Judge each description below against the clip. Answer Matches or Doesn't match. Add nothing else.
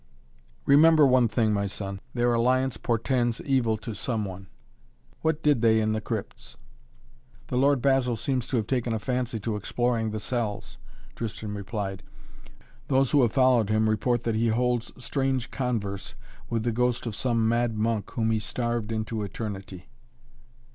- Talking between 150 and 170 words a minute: Matches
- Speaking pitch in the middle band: Doesn't match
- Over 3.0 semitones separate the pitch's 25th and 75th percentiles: Doesn't match